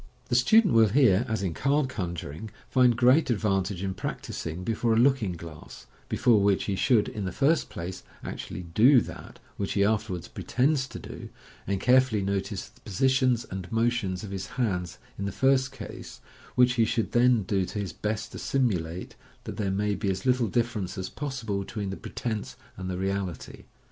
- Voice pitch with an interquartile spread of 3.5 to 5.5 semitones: Yes, average, 4.6 semitones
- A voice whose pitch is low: Yes, low, 105 Hz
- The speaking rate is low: No, average, 185 wpm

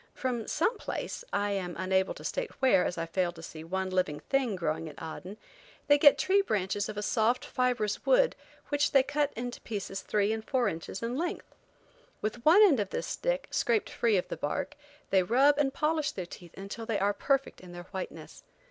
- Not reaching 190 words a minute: No, fast, 205 wpm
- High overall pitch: Yes, high, 215 Hz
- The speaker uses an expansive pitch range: Yes, wide, 7.0 semitones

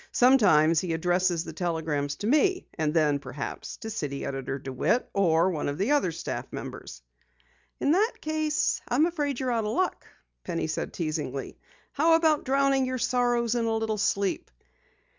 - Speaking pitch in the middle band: No, high, 210 Hz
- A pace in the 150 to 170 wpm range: Yes, average, 165 wpm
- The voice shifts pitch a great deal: Yes, wide, 9.0 semitones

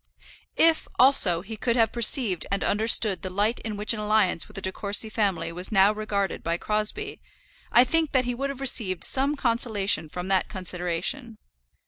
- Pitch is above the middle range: Yes, high, 215 Hz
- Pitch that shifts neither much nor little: Yes, average, 4.1 semitones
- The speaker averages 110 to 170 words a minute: No, average, 180 wpm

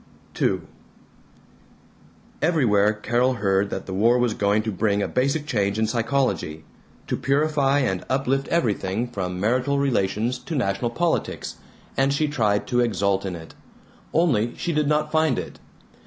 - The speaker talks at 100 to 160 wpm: Yes, average, 150 wpm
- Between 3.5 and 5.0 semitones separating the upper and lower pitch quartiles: No, wide, 5.5 semitones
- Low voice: Yes, low, 120 Hz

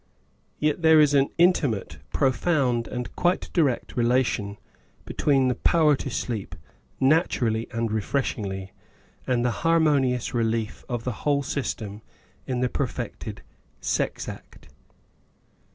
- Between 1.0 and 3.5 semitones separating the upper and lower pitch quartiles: No, average, 4.1 semitones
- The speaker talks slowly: Yes, slow, 125 wpm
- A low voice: Yes, low, 125 Hz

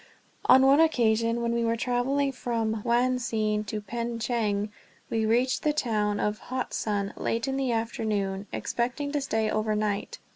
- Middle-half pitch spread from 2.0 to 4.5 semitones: Yes, average, 2.8 semitones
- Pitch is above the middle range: Yes, high, 230 Hz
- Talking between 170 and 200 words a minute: No, average, 150 wpm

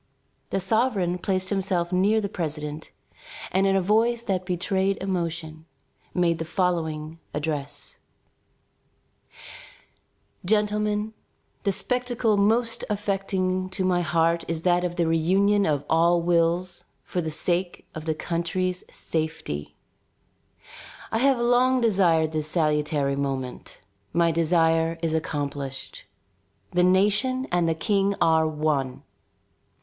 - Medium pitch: Yes, medium, 175 Hz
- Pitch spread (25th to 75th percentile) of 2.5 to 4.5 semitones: Yes, average, 3.7 semitones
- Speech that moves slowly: Yes, slow, 120 wpm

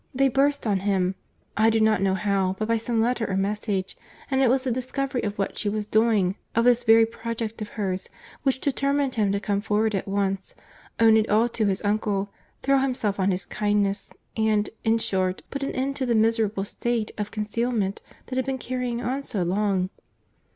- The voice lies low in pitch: No, high, 220 Hz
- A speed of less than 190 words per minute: No, average, 200 wpm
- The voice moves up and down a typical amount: Yes, average, 3.3 semitones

